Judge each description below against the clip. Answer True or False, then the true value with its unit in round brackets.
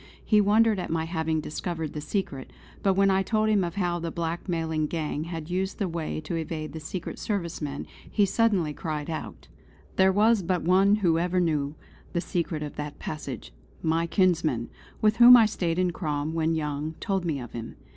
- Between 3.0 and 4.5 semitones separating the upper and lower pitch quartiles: True (3.5 semitones)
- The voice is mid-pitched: True (170 Hz)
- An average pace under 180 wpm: False (195 wpm)